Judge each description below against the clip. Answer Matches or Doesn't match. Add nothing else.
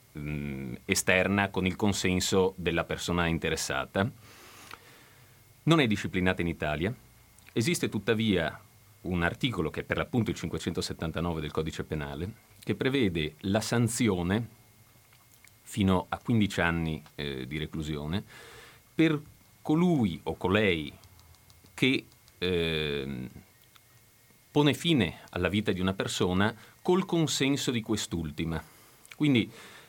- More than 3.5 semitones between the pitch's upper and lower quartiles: Matches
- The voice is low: Matches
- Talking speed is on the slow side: Matches